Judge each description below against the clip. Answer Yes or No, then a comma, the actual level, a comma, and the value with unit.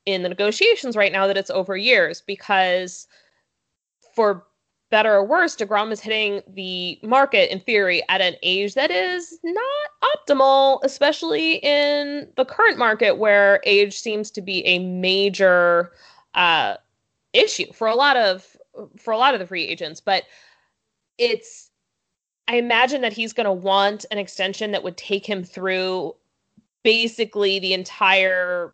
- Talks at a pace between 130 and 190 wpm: Yes, average, 150 wpm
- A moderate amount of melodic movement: No, wide, 6.0 semitones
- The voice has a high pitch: Yes, high, 205 Hz